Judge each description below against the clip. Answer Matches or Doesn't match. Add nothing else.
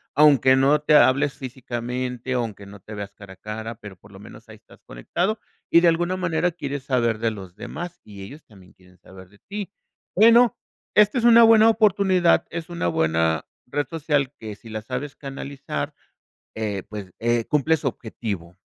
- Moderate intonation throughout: Doesn't match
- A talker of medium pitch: Doesn't match